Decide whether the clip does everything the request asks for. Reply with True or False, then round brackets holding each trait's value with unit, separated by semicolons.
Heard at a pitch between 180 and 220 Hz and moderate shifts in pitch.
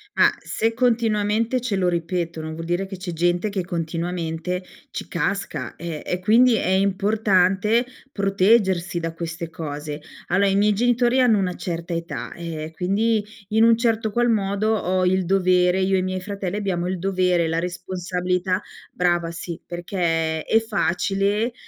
True (185 Hz; 3.3 semitones)